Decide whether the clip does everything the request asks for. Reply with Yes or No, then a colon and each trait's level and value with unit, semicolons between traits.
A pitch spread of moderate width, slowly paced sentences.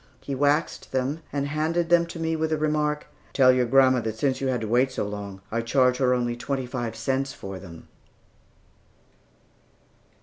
No: average, 3.7 semitones; average, 180 wpm